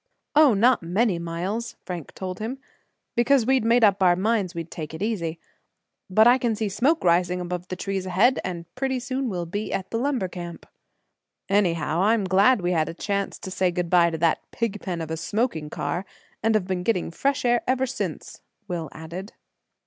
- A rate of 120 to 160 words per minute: No, average, 195 wpm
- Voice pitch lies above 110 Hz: Yes, high, 190 Hz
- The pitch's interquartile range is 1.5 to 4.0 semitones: No, average, 5.0 semitones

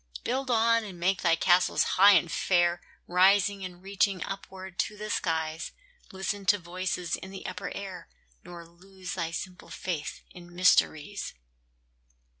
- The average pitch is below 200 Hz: Yes, medium, 185 Hz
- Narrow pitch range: Yes, narrow, 2.2 semitones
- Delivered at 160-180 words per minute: No, average, 145 wpm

